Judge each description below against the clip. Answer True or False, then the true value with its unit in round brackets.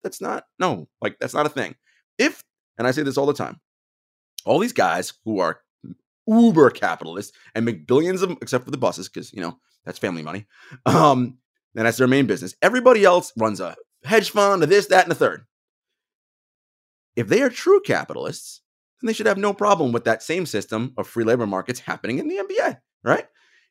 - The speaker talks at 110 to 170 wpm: False (200 wpm)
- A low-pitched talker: False (150 Hz)